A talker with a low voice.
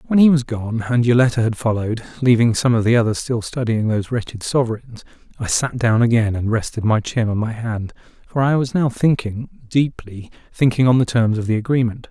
Yes: low, 120 Hz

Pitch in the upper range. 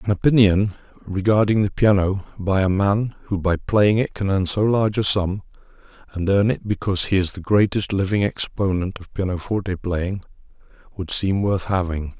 No: low, 100 Hz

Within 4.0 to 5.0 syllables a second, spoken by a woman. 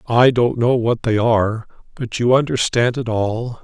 No: 4.4 syllables/s; male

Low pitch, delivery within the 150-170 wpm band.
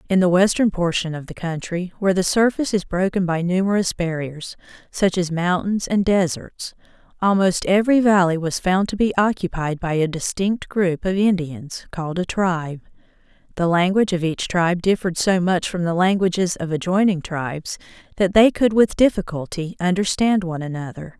No: medium, 180 Hz; average, 165 wpm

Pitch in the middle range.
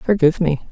Yes: medium, 165 Hz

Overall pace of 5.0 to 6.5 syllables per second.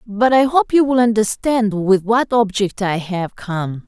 No: 4.0 syllables/s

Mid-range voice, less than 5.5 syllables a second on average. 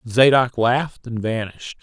No: low, 120 Hz; 4.8 syllables/s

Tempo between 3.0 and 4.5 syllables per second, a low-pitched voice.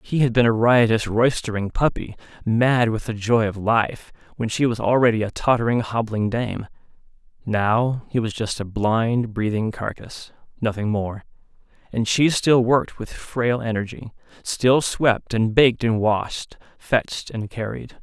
Yes: 4.4 syllables/s; low, 115 Hz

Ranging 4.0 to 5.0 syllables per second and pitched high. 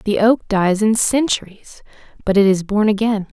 Yes: 4.5 syllables/s; high, 210 Hz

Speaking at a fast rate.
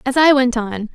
Yes: fast, 255 wpm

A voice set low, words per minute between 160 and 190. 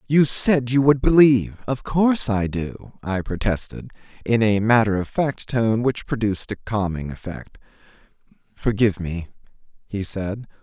No: low, 115 Hz; average, 145 wpm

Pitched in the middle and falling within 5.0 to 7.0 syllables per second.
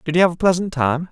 Yes: medium, 165 Hz; 6.9 syllables/s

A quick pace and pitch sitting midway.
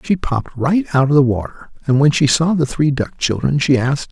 Yes: fast, 250 wpm; medium, 145 Hz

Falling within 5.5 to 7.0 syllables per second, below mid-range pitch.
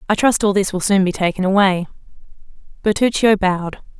No: 5.9 syllables/s; high, 195 Hz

